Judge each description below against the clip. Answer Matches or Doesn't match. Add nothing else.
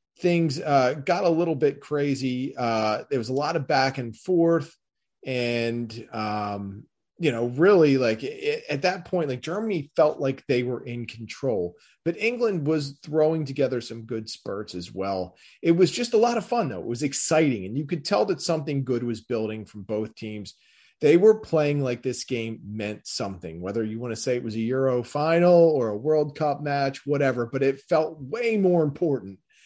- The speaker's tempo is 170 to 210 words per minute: Matches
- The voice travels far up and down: Matches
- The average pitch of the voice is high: Doesn't match